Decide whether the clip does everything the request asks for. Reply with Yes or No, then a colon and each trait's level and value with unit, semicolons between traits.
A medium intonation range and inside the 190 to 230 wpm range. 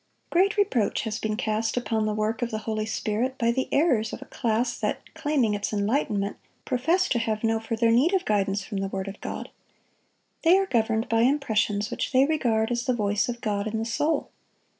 Yes: average, 3.3 semitones; fast, 205 wpm